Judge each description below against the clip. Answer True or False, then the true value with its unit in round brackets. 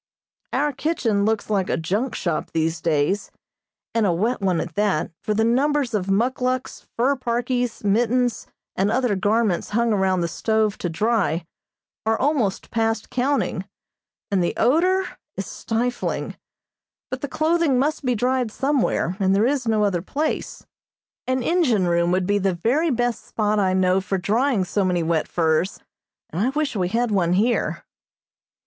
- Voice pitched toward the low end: False (220 Hz)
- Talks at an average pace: True (165 wpm)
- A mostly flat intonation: False (5.1 semitones)